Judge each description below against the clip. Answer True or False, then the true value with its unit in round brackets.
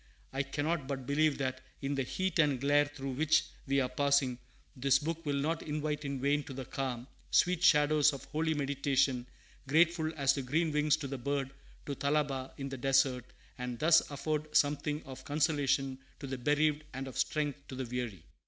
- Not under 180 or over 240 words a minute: True (190 wpm)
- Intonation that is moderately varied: False (2.2 semitones)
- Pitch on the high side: False (140 Hz)